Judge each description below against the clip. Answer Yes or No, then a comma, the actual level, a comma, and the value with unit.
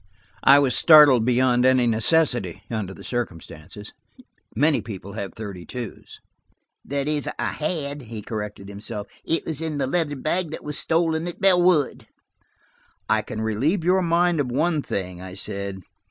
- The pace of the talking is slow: No, average, 155 wpm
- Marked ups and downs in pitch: Yes, wide, 7.2 semitones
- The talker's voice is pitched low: Yes, low, 130 Hz